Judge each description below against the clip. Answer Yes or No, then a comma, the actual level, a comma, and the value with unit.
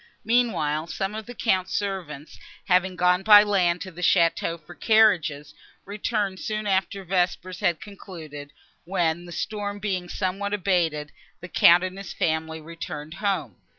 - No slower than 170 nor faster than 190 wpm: No, average, 150 wpm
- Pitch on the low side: No, medium, 180 Hz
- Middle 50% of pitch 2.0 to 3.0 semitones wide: No, average, 3.4 semitones